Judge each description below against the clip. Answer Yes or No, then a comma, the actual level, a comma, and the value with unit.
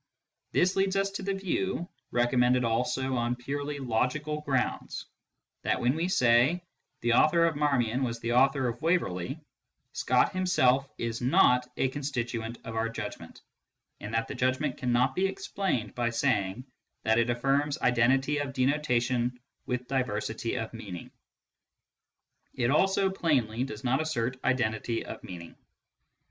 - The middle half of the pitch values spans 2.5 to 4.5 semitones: Yes, average, 3.9 semitones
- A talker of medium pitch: No, low, 125 Hz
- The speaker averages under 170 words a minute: Yes, average, 145 wpm